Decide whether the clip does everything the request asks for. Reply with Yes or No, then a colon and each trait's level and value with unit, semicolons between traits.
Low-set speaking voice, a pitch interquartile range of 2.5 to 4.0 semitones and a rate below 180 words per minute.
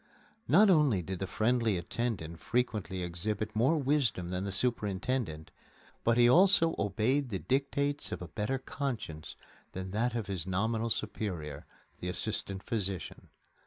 No: low, 110 Hz; average, 5.2 semitones; average, 140 wpm